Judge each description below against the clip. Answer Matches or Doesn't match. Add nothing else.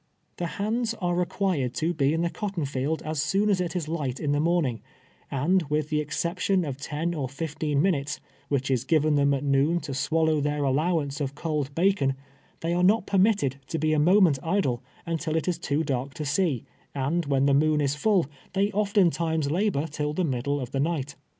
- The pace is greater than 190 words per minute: Matches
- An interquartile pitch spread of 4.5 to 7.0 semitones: Doesn't match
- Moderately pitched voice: Matches